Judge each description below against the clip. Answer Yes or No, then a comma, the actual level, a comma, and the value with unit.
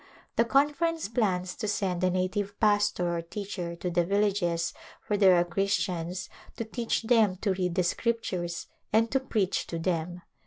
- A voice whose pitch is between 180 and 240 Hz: Yes, high, 190 Hz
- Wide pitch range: No, average, 3.6 semitones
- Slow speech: No, average, 165 wpm